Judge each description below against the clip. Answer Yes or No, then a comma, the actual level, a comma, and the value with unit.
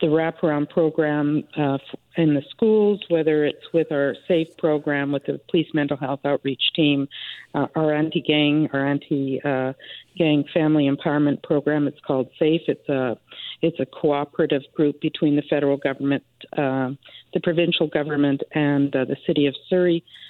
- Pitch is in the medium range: Yes, medium, 150 Hz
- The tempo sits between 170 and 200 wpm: No, average, 150 wpm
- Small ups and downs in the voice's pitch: Yes, narrow, 2.3 semitones